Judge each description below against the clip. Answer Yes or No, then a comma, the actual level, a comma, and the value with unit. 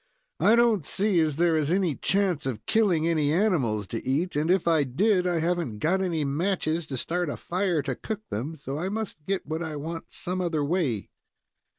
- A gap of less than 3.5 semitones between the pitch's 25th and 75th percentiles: No, average, 4.1 semitones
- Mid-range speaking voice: Yes, medium, 165 Hz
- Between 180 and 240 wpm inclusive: Yes, fast, 205 wpm